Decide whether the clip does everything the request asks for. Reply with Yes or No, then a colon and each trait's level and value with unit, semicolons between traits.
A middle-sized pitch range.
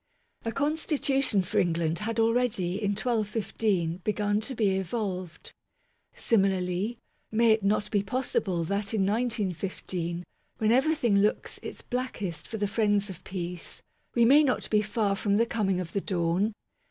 Yes: average, 3.5 semitones